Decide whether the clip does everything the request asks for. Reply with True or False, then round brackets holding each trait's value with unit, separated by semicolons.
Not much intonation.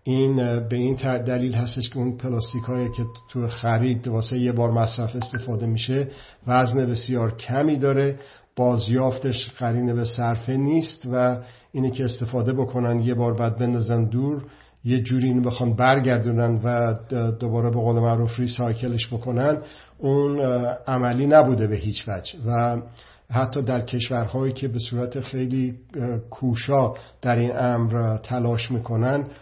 True (1.6 semitones)